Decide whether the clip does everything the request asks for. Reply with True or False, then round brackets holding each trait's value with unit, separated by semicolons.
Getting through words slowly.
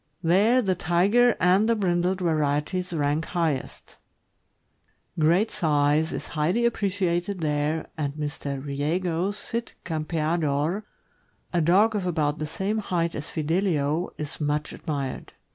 True (125 wpm)